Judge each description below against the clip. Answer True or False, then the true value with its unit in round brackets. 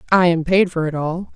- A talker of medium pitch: True (170 Hz)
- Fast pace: True (265 wpm)